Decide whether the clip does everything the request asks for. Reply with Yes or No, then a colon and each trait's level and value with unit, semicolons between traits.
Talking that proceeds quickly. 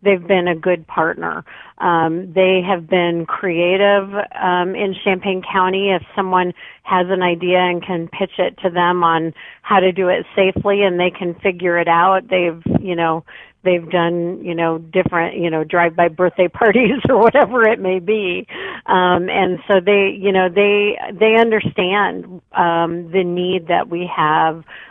No: average, 170 wpm